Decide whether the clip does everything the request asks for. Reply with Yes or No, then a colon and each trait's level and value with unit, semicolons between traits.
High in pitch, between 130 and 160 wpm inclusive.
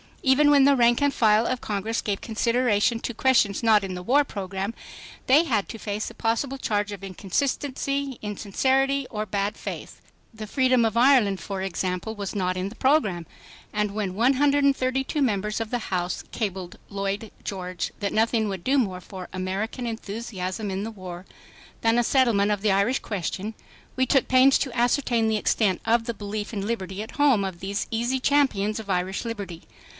No: high, 215 Hz; average, 180 wpm